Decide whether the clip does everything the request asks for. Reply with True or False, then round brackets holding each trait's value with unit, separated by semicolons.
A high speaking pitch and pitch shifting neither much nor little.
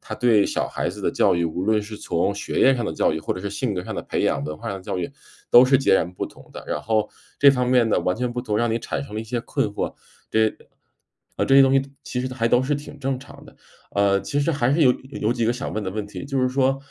False (115 Hz; 4.3 semitones)